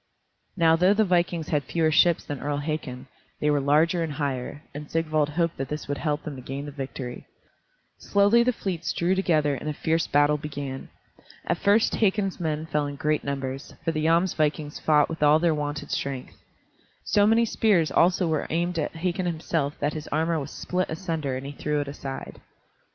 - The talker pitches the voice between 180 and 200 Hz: No, medium, 155 Hz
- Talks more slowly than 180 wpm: No, average, 195 wpm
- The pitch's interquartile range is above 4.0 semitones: No, average, 2.9 semitones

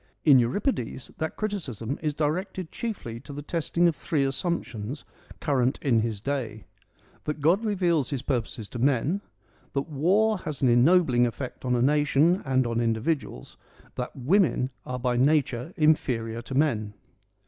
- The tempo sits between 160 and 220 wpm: No, average, 150 wpm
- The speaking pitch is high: No, medium, 140 Hz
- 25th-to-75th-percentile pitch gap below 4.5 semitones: No, average, 5.0 semitones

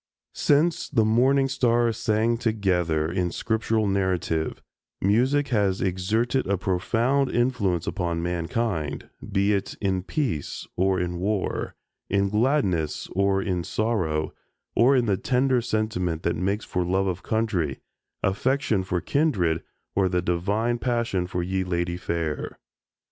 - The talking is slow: Yes, slow, 130 wpm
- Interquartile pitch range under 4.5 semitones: No, average, 4.8 semitones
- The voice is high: No, low, 100 Hz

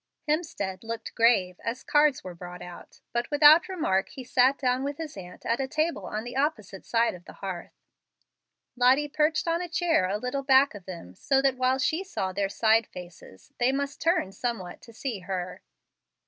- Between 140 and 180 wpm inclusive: No, average, 190 wpm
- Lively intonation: Yes, wide, 6.9 semitones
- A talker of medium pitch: No, high, 245 Hz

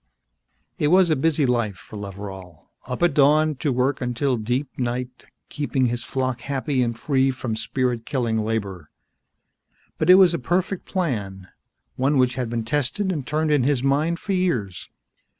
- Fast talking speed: No, average, 170 wpm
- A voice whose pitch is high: No, low, 130 Hz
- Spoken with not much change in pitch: No, average, 4.3 semitones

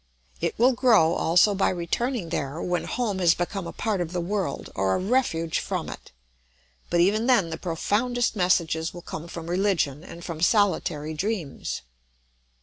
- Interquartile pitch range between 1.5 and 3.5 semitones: No, average, 4.2 semitones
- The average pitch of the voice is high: No, medium, 175 Hz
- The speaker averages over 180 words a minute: No, average, 165 wpm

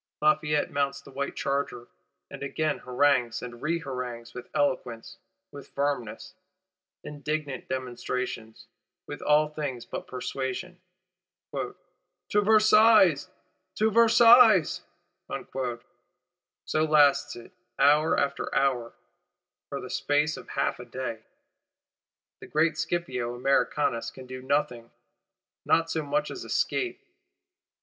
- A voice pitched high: No, medium, 140 Hz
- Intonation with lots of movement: No, average, 3.6 semitones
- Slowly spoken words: Yes, slow, 110 wpm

